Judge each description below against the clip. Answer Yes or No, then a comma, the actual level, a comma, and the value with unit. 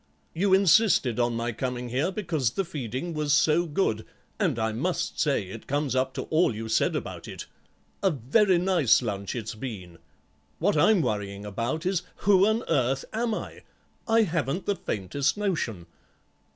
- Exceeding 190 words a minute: No, average, 165 wpm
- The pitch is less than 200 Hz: Yes, medium, 140 Hz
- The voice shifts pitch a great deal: Yes, wide, 8.1 semitones